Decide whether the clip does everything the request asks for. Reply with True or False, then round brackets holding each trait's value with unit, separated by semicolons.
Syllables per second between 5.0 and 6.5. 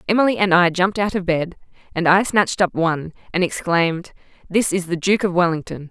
True (6.0 syllables/s)